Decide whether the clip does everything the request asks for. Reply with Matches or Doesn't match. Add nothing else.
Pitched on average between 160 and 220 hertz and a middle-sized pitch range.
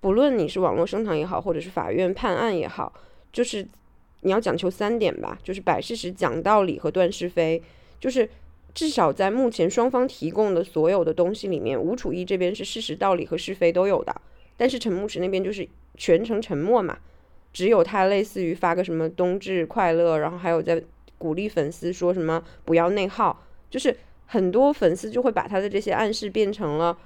Matches